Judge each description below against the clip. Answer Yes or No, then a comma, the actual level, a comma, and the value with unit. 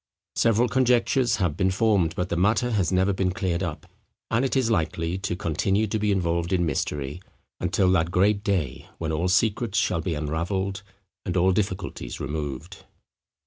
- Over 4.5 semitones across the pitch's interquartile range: No, average, 3.8 semitones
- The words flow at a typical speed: Yes, average, 170 wpm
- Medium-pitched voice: No, very low, 95 Hz